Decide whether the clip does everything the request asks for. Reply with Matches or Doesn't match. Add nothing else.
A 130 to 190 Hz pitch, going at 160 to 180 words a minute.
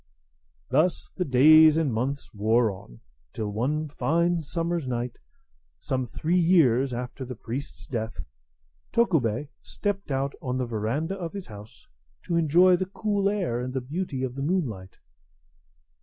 Doesn't match